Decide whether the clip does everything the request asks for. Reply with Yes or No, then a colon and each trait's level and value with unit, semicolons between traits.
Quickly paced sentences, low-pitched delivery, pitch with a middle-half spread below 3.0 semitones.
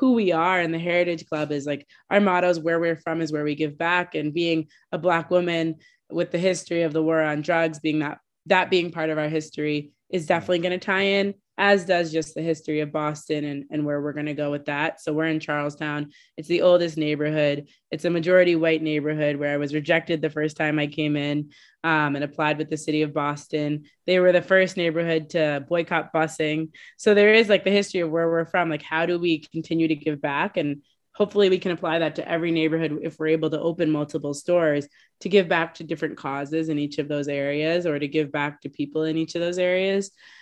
No: fast, 235 wpm; medium, 160 Hz; narrow, 2.5 semitones